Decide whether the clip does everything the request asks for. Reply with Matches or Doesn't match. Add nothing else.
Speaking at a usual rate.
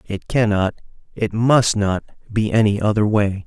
Matches